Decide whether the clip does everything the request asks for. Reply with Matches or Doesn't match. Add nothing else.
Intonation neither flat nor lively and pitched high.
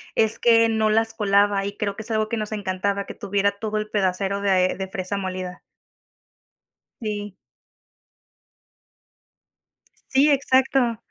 Doesn't match